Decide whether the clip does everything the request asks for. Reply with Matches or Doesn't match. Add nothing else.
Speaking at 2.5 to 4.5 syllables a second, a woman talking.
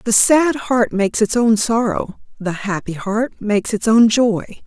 Matches